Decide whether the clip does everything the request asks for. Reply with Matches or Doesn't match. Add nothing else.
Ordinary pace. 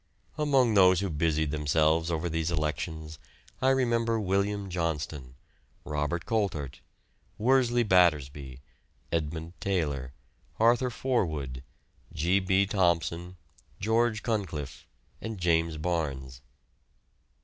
Doesn't match